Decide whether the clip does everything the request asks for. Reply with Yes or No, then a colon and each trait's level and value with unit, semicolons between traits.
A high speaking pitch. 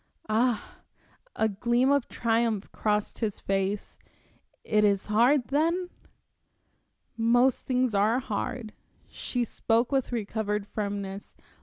Yes: high, 225 Hz